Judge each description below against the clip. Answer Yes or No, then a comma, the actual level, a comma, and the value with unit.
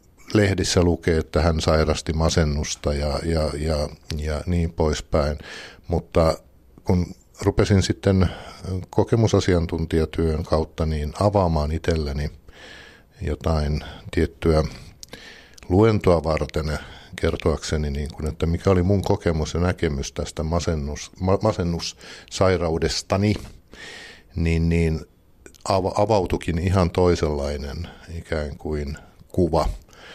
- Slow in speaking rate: Yes, slow, 90 wpm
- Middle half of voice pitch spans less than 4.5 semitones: Yes, average, 2.8 semitones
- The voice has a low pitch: Yes, very low, 85 Hz